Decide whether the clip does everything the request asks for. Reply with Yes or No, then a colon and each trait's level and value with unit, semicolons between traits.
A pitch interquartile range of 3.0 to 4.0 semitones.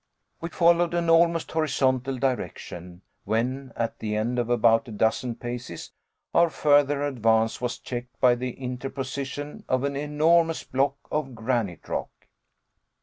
Yes: average, 3.5 semitones